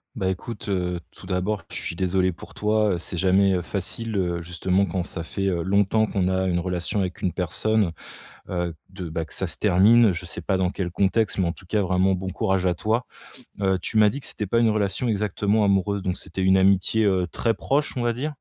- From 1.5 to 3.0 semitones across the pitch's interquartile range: Yes, narrow, 2.5 semitones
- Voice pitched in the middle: No, very low, 95 Hz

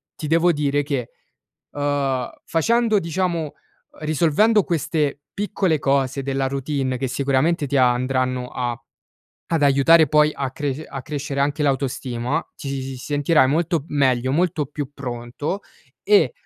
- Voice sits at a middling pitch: Yes, medium, 145 Hz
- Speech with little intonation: No, average, 3.1 semitones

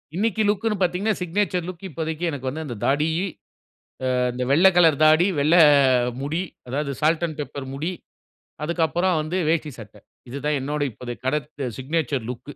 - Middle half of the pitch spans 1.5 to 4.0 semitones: Yes, average, 3.7 semitones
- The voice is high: No, medium, 155 Hz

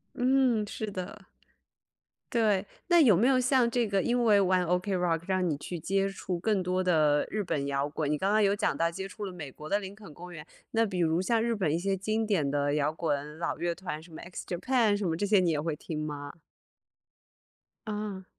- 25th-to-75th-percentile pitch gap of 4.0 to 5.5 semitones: Yes, average, 4.5 semitones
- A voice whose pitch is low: No, medium, 185 Hz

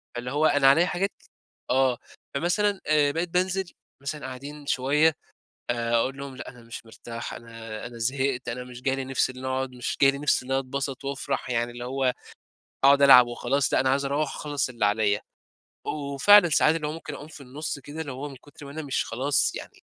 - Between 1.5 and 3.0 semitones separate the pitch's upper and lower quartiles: Yes, average, 2.7 semitones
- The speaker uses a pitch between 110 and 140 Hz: Yes, low, 135 Hz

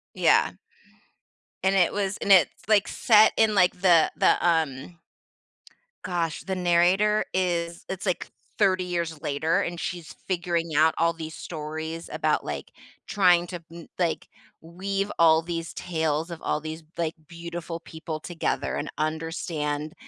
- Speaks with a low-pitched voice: No, medium, 170 Hz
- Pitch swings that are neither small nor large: No, narrow, 2.3 semitones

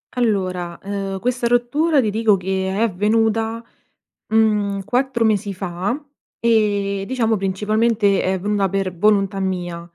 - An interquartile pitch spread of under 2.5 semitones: No, average, 2.9 semitones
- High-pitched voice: Yes, high, 205 Hz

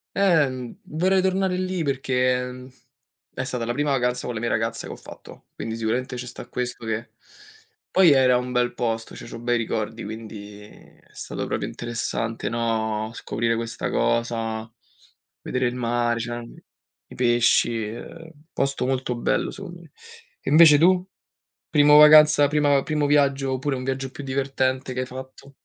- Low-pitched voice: Yes, low, 125 Hz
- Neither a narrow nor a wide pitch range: Yes, average, 3.5 semitones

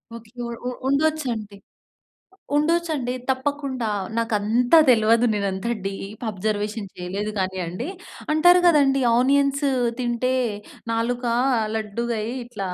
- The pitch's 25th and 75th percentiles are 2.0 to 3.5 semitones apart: No, average, 4.5 semitones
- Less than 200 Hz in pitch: No, high, 235 Hz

